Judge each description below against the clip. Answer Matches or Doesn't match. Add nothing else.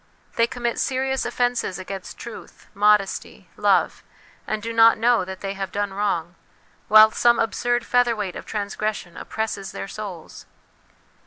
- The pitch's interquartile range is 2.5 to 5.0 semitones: Matches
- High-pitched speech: Matches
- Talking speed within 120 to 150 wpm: Matches